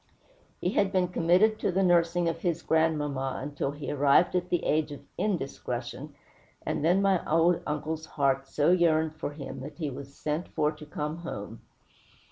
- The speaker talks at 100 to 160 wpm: No, average, 180 wpm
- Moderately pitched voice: Yes, medium, 155 Hz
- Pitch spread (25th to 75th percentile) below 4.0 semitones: Yes, average, 3.3 semitones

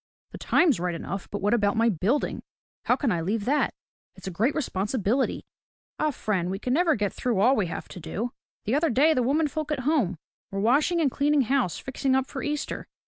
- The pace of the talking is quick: Yes, fast, 215 wpm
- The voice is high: Yes, high, 245 Hz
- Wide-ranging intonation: Yes, wide, 6.3 semitones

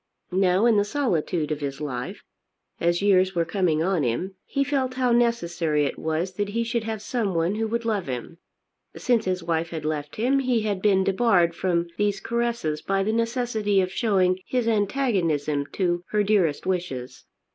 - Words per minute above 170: Yes, average, 180 wpm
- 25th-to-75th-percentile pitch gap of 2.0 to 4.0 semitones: No, average, 5.2 semitones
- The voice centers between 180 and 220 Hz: Yes, high, 190 Hz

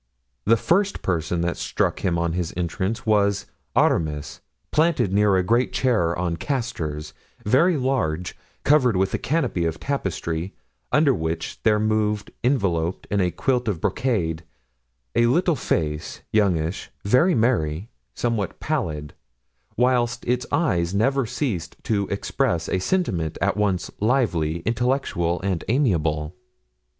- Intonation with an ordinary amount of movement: No, wide, 6.7 semitones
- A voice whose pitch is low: Yes, low, 100 Hz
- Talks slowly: Yes, slow, 130 wpm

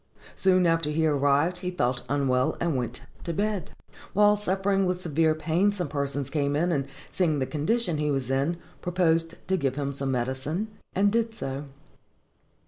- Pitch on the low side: No, medium, 160 Hz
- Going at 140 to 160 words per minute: No, average, 170 wpm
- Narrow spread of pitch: No, average, 4.7 semitones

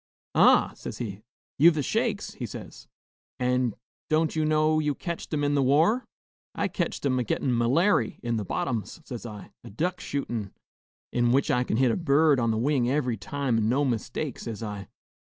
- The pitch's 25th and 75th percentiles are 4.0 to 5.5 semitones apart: Yes, average, 4.7 semitones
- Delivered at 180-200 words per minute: Yes, average, 190 wpm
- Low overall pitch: Yes, low, 130 Hz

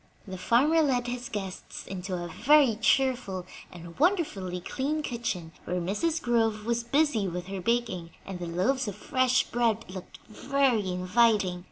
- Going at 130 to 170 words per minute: Yes, average, 155 wpm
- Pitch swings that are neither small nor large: No, wide, 5.8 semitones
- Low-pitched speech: No, high, 225 Hz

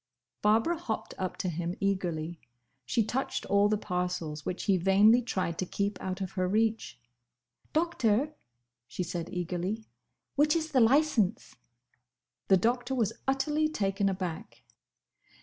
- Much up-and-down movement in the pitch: No, average, 5.0 semitones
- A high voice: Yes, high, 200 Hz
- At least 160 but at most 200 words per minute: No, slow, 135 wpm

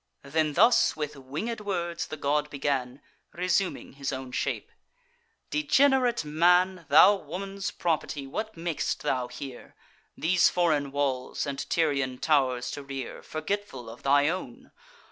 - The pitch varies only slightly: No, average, 4.8 semitones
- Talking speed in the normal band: No, slow, 130 wpm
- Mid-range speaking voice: Yes, medium, 150 Hz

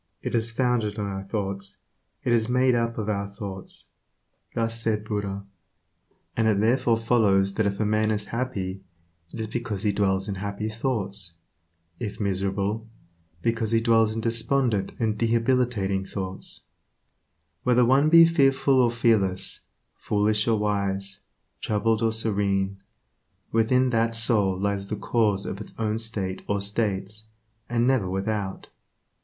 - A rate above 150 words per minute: No, average, 145 wpm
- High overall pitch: No, low, 110 Hz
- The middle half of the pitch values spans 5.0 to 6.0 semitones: No, average, 2.7 semitones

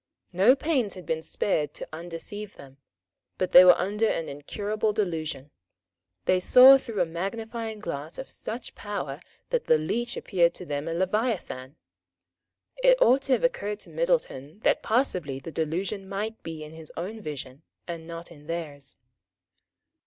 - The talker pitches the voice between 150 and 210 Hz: Yes, medium, 185 Hz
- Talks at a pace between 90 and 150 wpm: No, average, 160 wpm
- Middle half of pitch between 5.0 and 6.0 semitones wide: Yes, wide, 5.6 semitones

